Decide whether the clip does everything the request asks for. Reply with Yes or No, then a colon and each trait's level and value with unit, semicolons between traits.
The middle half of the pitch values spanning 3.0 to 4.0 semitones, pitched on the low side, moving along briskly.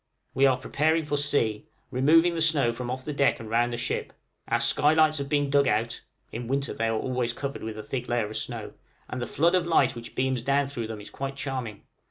Yes: average, 3.5 semitones; low, 130 Hz; fast, 240 wpm